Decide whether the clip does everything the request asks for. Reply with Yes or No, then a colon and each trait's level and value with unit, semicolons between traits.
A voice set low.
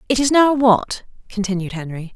No: high, 220 Hz